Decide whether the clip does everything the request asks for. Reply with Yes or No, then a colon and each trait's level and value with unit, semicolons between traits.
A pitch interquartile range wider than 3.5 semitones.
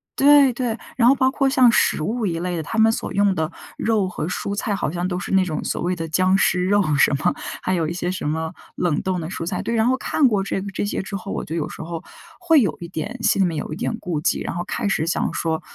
Yes: average, 4.9 semitones